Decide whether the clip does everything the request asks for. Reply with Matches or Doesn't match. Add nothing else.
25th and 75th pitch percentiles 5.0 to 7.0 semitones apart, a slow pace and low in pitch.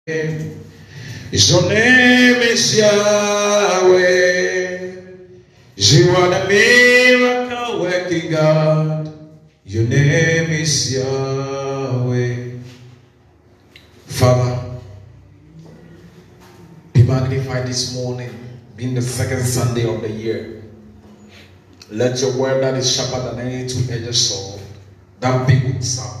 Matches